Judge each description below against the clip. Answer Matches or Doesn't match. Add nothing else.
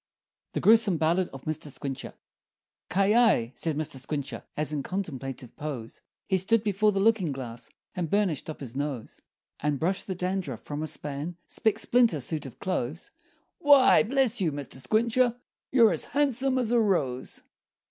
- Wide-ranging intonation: Matches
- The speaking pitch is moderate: Matches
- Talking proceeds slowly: Doesn't match